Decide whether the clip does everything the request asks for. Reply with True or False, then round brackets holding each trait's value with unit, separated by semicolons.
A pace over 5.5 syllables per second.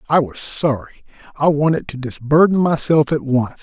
False (5.1 syllables/s)